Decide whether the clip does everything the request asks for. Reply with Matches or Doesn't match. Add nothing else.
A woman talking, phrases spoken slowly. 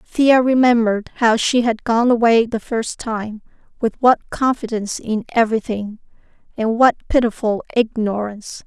Matches